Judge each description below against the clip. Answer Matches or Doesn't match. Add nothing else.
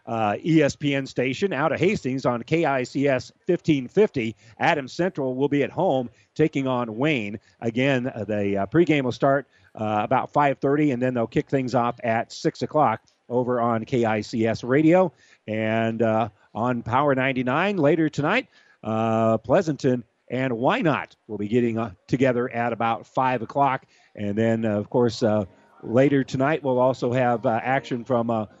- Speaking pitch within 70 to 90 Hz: Doesn't match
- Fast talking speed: Doesn't match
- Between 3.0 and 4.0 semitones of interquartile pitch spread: Matches